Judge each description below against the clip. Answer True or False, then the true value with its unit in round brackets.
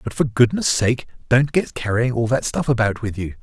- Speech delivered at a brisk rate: True (230 wpm)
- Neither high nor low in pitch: False (120 Hz)